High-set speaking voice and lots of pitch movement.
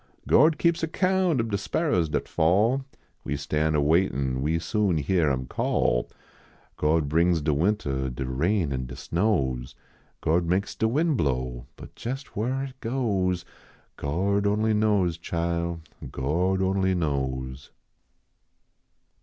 No: very low, 85 Hz; wide, 6.9 semitones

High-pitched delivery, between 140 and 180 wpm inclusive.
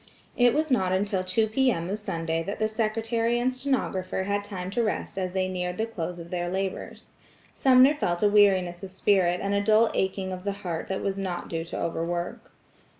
No: high, 195 Hz; fast, 205 wpm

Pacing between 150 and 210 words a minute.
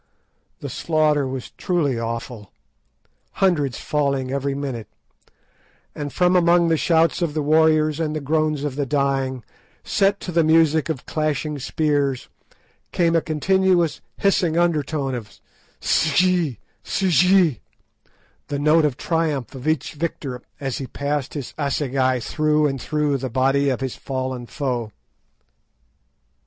No: slow, 135 wpm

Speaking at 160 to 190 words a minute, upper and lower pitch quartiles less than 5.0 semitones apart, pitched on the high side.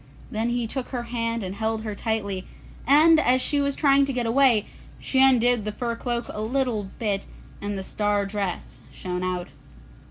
Yes: average, 185 wpm; average, 3.7 semitones; high, 230 Hz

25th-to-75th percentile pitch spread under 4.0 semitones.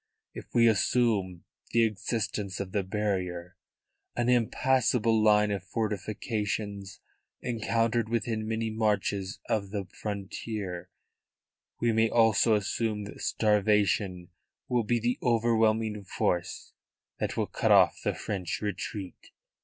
Yes: narrow, 2.4 semitones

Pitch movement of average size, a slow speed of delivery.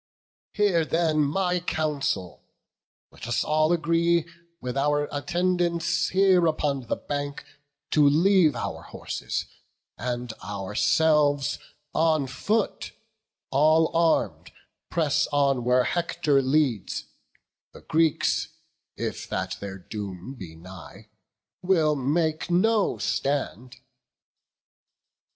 Yes: average, 4.7 semitones; slow, 100 wpm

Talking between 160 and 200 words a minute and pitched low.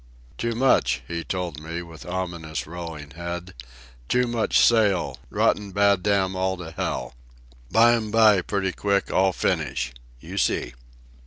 No: average, 140 wpm; very low, 95 Hz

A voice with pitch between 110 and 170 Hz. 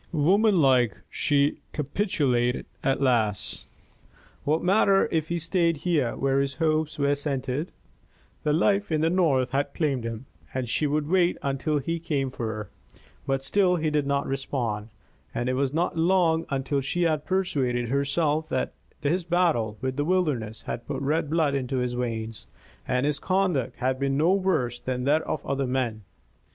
Yes: medium, 140 Hz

